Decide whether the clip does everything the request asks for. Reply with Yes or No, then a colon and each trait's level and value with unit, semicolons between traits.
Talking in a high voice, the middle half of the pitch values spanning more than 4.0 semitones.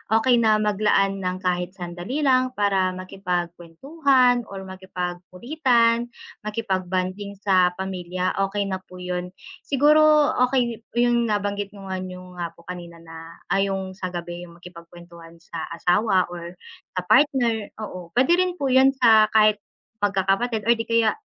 Yes: high, 195 Hz; average, 4.4 semitones